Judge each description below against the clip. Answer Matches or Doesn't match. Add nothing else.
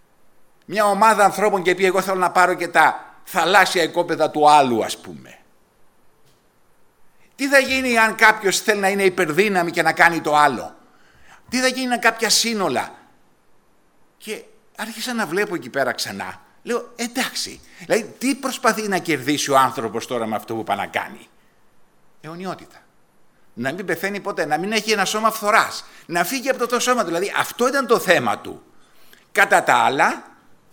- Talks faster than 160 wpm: Matches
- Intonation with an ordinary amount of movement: Doesn't match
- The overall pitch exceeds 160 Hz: Matches